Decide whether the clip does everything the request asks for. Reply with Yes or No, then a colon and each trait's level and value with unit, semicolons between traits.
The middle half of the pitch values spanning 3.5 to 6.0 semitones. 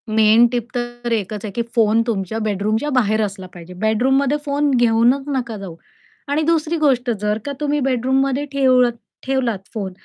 Yes: average, 4.0 semitones